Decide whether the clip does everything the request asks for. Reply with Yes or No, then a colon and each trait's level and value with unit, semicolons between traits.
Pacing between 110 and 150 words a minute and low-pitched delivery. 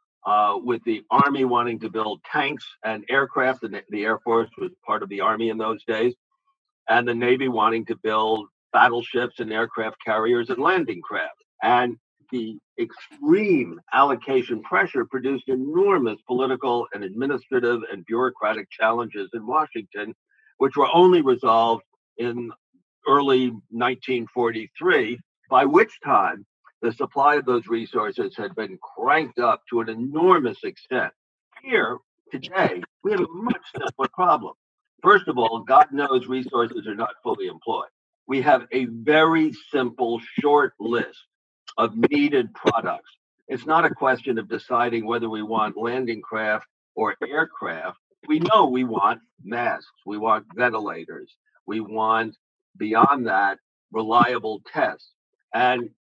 Yes: average, 140 wpm; low, 125 Hz